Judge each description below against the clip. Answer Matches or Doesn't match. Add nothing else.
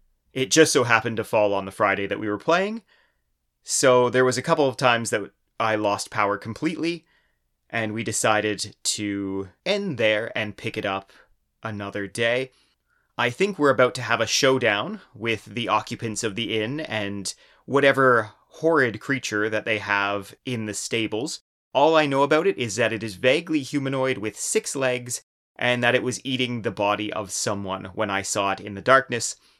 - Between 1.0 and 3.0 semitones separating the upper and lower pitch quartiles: Doesn't match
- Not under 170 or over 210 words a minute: Matches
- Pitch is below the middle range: Matches